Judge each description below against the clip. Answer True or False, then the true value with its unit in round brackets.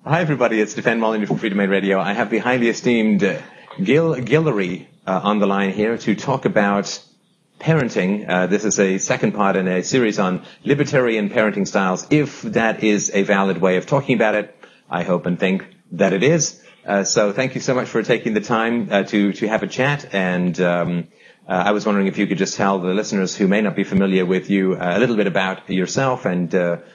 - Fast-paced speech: True (220 wpm)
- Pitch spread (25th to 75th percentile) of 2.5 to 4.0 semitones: True (3.5 semitones)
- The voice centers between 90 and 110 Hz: True (100 Hz)